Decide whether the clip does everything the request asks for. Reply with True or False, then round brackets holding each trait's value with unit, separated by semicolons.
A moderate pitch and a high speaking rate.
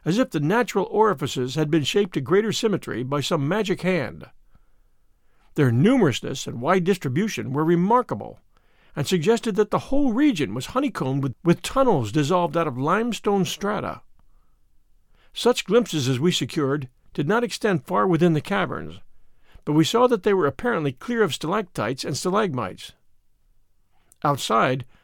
False (175 Hz; 150 wpm)